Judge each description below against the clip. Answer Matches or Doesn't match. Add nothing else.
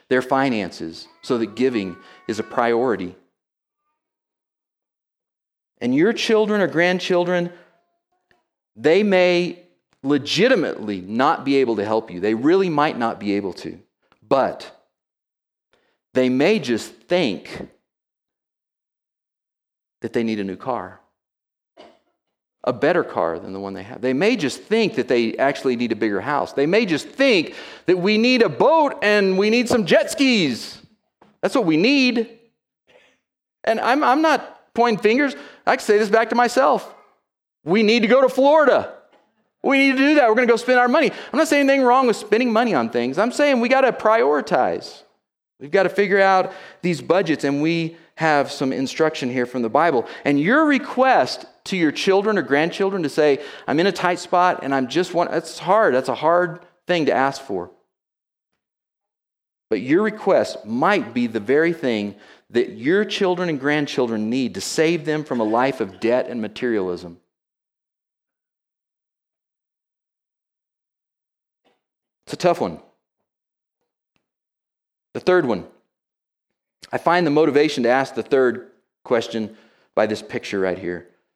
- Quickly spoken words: Doesn't match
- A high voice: Doesn't match